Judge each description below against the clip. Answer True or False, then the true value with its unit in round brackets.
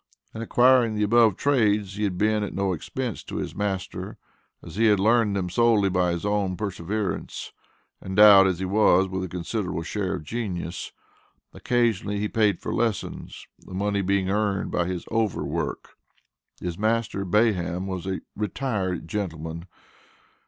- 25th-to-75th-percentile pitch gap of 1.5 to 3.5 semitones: True (2.8 semitones)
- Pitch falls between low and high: False (100 Hz)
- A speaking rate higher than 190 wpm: False (160 wpm)